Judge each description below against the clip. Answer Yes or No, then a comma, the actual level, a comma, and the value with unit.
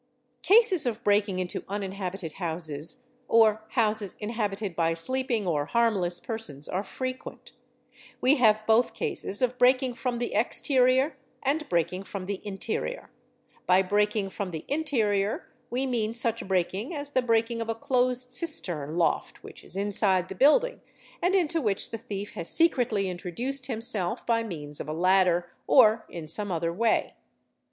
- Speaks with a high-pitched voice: Yes, high, 215 Hz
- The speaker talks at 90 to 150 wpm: No, average, 160 wpm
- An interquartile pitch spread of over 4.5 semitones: Yes, average, 5.2 semitones